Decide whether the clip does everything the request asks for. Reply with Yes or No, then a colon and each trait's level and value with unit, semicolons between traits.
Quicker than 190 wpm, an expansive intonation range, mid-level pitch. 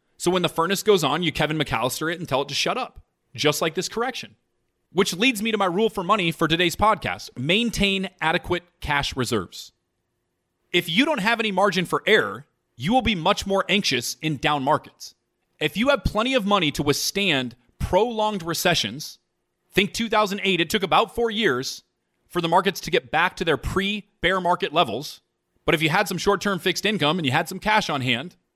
Yes: fast, 205 wpm; wide, 5.7 semitones; medium, 175 Hz